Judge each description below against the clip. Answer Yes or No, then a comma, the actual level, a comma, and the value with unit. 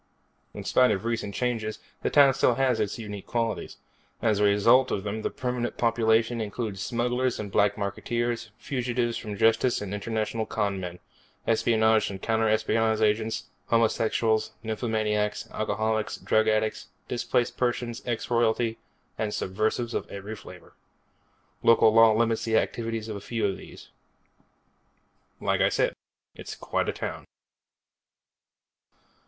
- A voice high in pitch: No, low, 110 Hz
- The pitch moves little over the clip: Yes, narrow, 1.7 semitones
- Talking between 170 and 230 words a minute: No, slow, 135 wpm